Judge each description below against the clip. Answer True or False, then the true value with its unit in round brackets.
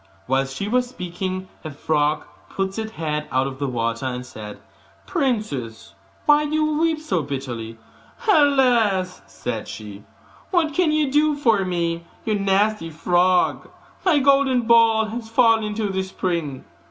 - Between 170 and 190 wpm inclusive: False (150 wpm)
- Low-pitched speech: False (195 Hz)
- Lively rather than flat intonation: True (8.9 semitones)